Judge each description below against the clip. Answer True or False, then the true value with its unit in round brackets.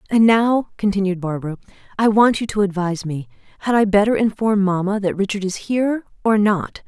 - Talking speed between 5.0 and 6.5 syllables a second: True (5.7 syllables/s)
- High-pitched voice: True (200 Hz)